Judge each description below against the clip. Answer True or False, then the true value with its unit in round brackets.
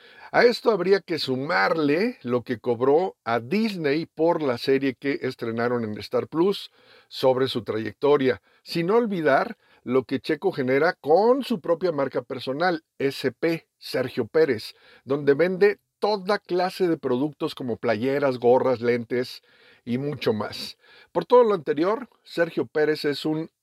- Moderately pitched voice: True (145 Hz)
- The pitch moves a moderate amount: False (5.9 semitones)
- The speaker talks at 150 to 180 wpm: False (140 wpm)